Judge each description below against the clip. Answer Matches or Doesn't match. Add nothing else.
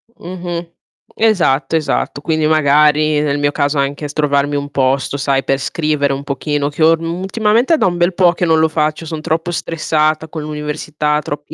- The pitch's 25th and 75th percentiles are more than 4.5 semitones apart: Doesn't match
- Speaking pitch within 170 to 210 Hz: Doesn't match